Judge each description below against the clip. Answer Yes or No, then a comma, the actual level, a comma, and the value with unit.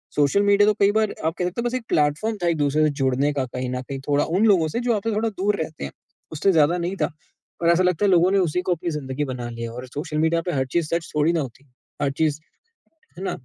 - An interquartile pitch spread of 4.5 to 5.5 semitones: Yes, average, 5.0 semitones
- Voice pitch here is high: No, medium, 160 Hz